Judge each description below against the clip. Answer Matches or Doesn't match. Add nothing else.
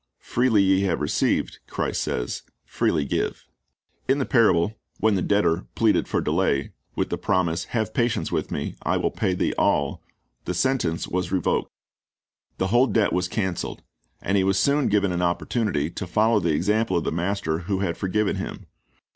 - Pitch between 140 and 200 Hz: Doesn't match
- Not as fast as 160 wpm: Doesn't match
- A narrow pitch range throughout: Doesn't match